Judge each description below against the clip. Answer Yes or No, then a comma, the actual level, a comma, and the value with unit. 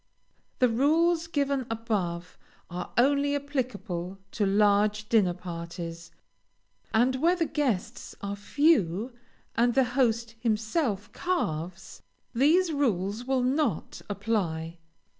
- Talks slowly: Yes, slow, 105 wpm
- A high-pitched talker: Yes, high, 225 Hz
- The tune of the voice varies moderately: No, wide, 6.5 semitones